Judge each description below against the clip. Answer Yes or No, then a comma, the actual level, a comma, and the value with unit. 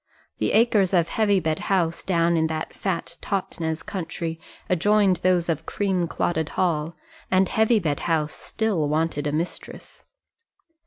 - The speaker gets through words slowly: Yes, slow, 125 wpm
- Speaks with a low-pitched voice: No, medium, 170 Hz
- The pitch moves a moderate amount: Yes, average, 3.2 semitones